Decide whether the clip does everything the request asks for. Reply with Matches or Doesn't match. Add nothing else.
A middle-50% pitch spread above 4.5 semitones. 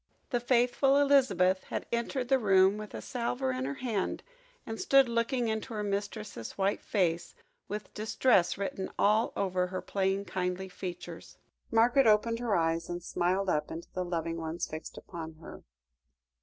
Matches